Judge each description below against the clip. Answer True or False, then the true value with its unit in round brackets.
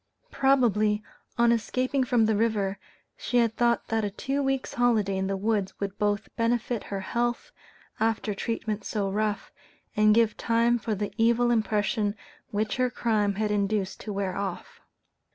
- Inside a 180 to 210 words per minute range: False (160 wpm)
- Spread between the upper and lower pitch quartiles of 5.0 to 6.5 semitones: False (2.4 semitones)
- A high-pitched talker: True (215 Hz)